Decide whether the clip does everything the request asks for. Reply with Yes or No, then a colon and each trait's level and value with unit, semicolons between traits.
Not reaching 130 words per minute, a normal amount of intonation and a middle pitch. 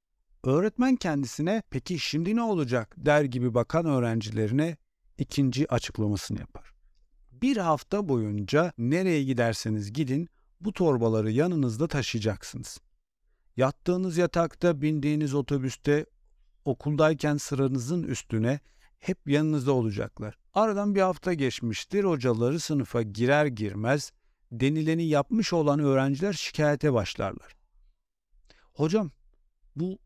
Yes: average, 100 wpm; average, 5.0 semitones; medium, 145 Hz